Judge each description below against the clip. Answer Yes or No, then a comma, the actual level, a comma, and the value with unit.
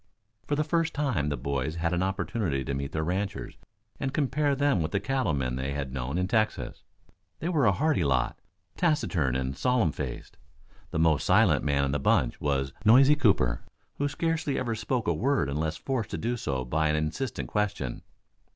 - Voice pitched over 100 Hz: No, very low, 90 Hz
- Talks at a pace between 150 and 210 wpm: Yes, average, 190 wpm